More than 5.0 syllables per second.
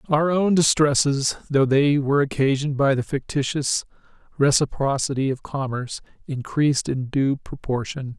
No: 4.9 syllables/s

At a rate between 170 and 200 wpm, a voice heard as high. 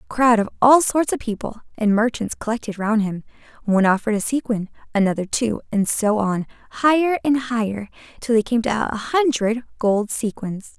Yes: average, 180 wpm; high, 225 Hz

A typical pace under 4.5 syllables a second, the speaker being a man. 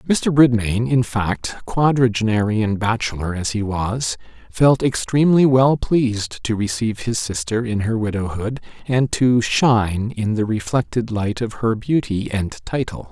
Yes: 4.3 syllables/s; male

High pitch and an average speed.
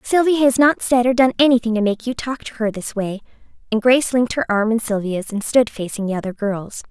No: high, 230 Hz; fast, 245 wpm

